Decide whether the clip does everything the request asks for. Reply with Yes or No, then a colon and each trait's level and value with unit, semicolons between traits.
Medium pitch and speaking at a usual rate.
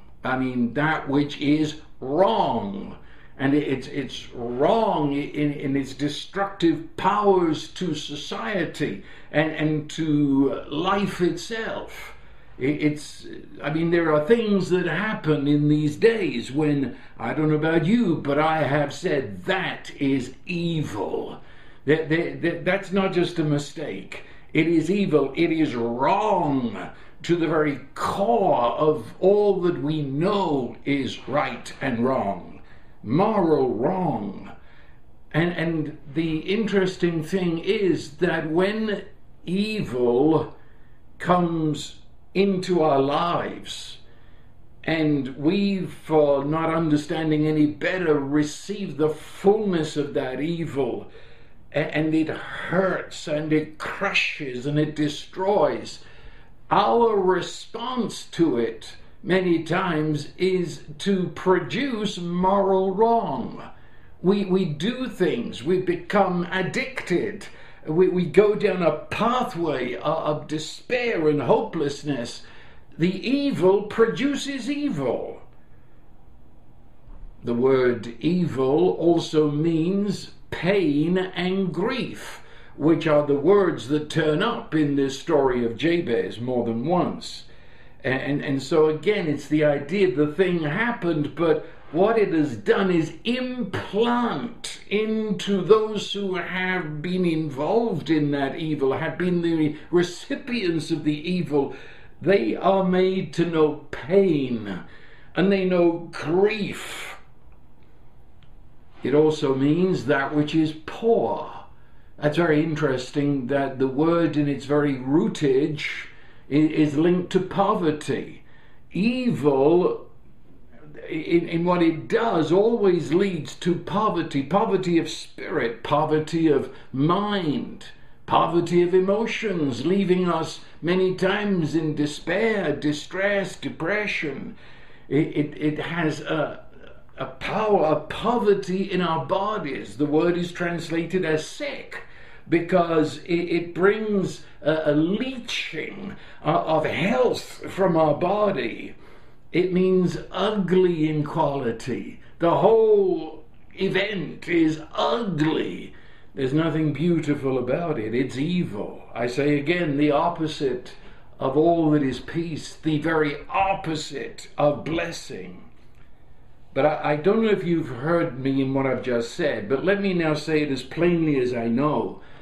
No: medium, 160 Hz; slow, 120 wpm